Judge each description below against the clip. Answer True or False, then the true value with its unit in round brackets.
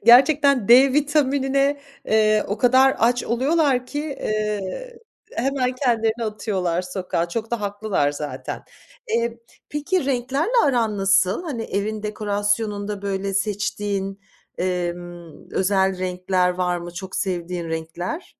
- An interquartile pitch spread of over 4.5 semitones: True (5.4 semitones)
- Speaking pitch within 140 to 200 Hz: False (210 Hz)